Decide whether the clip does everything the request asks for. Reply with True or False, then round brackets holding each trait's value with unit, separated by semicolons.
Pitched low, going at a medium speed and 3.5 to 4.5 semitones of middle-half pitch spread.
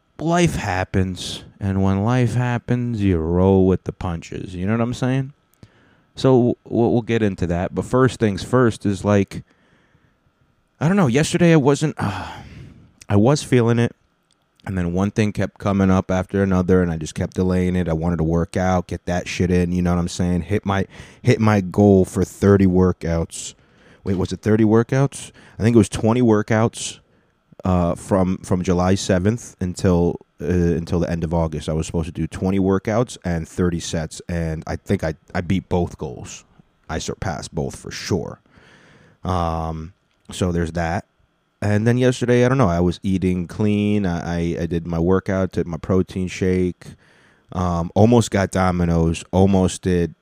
True (95 Hz; 180 wpm; 3.9 semitones)